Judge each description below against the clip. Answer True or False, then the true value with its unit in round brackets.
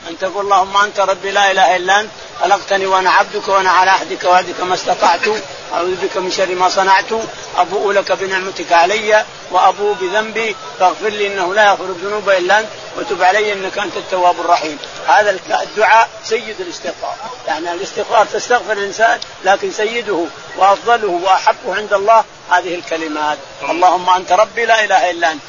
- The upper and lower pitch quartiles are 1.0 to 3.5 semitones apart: True (2.8 semitones)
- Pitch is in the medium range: False (195 Hz)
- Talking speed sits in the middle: False (160 wpm)